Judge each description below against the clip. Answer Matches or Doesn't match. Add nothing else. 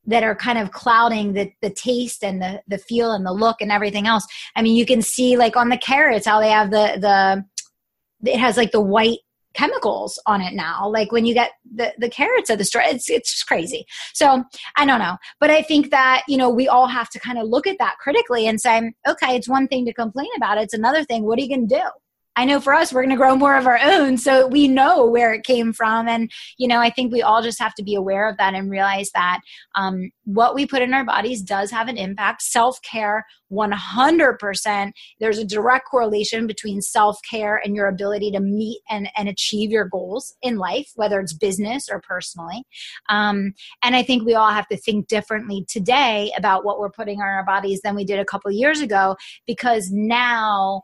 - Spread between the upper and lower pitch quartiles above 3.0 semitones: Matches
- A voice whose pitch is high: Matches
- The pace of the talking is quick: Matches